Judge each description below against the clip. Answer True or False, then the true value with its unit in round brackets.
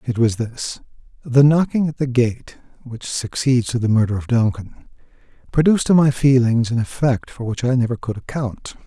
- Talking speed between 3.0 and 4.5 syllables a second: False (5.1 syllables/s)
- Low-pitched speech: True (125 Hz)